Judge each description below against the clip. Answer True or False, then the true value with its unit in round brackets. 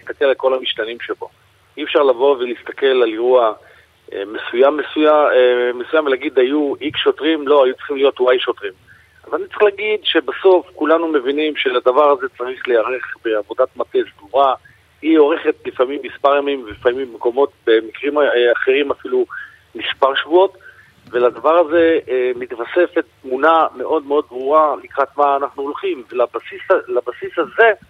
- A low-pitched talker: False (185 Hz)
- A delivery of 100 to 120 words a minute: False (140 wpm)